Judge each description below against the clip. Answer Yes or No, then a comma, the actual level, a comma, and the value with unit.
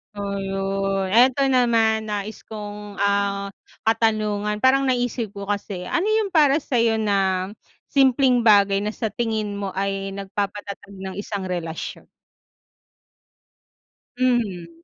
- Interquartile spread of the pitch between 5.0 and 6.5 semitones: No, average, 3.0 semitones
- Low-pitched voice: No, high, 205 Hz